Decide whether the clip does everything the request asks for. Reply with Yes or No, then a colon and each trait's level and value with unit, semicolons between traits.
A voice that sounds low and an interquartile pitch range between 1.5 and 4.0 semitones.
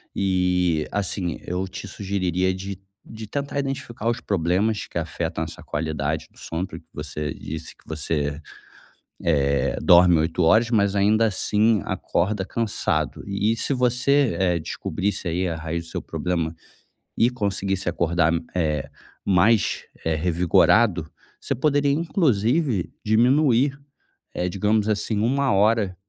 No: very low, 95 Hz; average, 4.8 semitones